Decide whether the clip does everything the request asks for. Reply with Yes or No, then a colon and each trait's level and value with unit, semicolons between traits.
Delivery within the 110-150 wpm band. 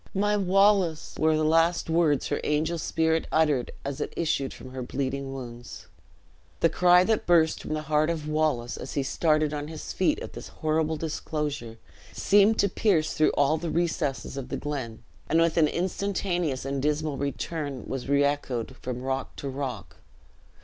No: average, 175 wpm